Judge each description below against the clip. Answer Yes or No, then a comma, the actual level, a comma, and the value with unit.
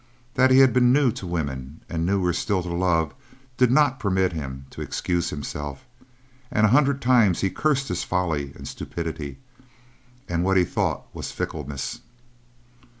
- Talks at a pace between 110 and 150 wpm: No, average, 160 wpm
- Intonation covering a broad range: Yes, wide, 7.7 semitones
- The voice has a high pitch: No, very low, 90 Hz